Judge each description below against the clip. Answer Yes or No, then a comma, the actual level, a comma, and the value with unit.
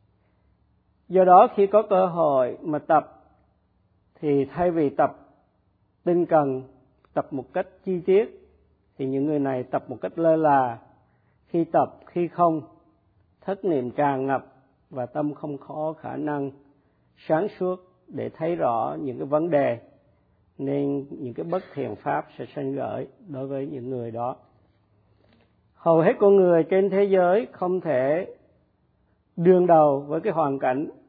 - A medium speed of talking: No, slow, 155 wpm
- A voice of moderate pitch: Yes, medium, 145 Hz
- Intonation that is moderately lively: No, wide, 5.8 semitones